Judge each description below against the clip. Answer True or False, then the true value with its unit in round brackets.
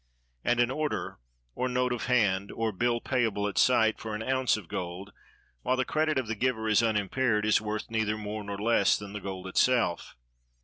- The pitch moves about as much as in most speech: True (3.4 semitones)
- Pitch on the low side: True (110 Hz)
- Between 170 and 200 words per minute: True (195 wpm)